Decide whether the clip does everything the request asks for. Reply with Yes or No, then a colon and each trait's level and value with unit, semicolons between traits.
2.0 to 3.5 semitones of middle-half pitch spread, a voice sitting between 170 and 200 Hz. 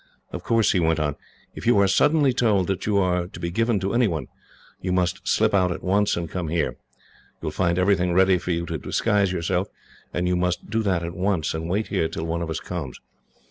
No: average, 2.9 semitones; very low, 90 Hz